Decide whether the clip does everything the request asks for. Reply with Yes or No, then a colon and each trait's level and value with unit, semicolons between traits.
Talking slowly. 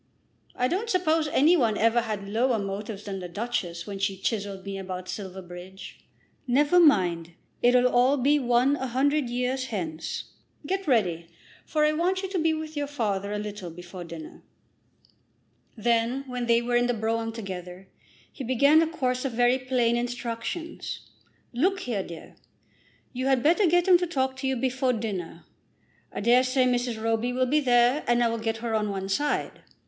No: average, 180 wpm